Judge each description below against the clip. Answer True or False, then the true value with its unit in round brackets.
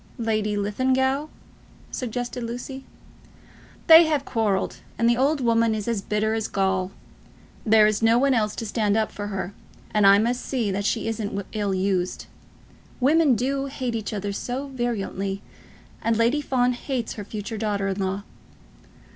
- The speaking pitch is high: True (225 Hz)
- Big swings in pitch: False (3.5 semitones)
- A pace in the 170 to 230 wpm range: False (160 wpm)